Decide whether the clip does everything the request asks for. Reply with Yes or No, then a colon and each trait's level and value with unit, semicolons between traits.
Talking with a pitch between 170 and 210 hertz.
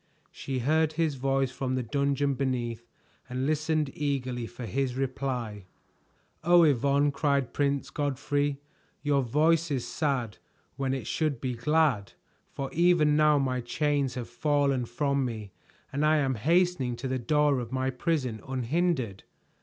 No: low, 135 Hz